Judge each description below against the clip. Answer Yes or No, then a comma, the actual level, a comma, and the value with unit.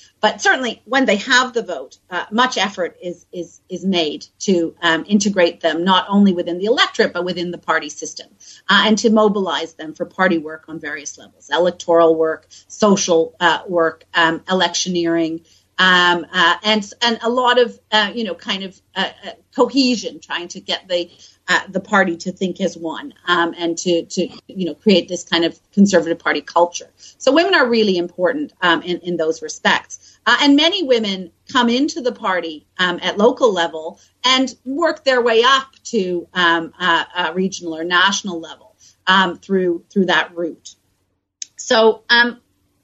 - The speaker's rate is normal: Yes, average, 180 wpm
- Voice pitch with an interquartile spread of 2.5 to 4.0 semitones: No, average, 4.9 semitones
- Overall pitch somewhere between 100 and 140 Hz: No, medium, 180 Hz